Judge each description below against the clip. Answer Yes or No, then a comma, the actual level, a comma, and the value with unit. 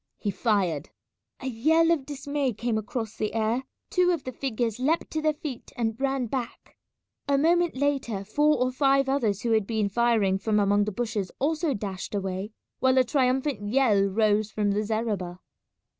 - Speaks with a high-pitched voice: Yes, high, 235 Hz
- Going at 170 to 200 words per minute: Yes, average, 175 wpm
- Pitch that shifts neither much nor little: Yes, average, 4.7 semitones